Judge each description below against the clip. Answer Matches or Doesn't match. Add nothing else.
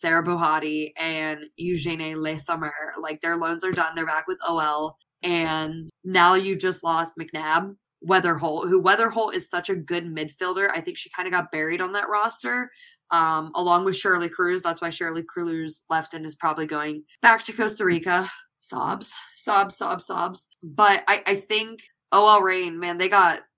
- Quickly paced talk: Doesn't match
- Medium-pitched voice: Matches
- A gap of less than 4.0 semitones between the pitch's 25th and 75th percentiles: Matches